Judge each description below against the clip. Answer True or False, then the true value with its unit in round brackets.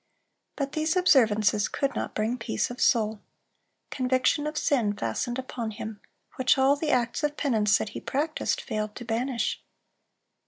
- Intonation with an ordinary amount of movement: True (4.4 semitones)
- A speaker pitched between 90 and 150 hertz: False (245 Hz)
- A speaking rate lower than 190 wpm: True (155 wpm)